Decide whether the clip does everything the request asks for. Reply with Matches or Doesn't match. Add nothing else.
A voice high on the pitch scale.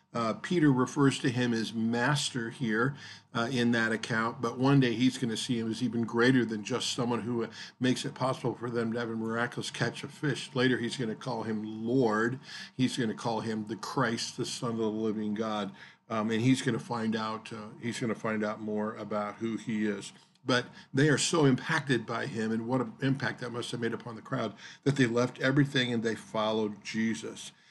Doesn't match